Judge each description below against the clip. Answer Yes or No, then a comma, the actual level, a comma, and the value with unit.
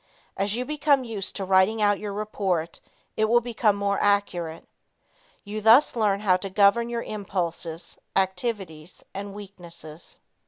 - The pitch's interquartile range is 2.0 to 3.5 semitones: Yes, average, 2.8 semitones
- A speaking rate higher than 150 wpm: No, average, 145 wpm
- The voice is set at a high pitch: Yes, high, 200 Hz